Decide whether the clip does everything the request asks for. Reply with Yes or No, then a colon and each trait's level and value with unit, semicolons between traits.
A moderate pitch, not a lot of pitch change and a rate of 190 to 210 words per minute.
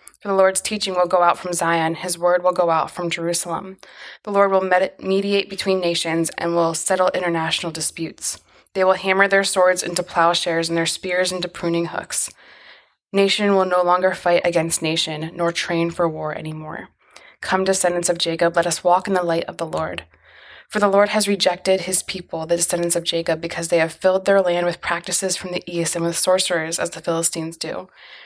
Yes: medium, 175 Hz; narrow, 2.0 semitones; average, 200 wpm